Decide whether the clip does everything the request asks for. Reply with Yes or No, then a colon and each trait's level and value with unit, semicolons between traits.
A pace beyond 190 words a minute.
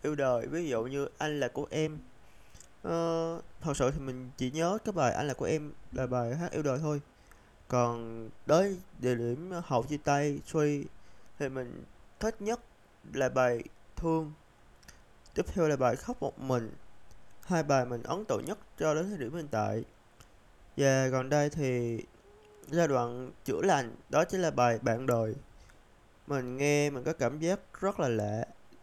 No: average, 175 wpm